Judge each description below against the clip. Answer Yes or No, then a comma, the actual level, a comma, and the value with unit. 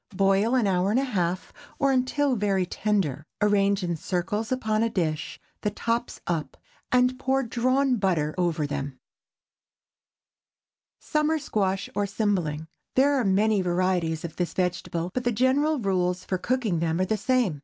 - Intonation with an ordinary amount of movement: No, wide, 5.8 semitones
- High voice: Yes, high, 200 Hz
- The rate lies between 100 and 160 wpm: Yes, average, 155 wpm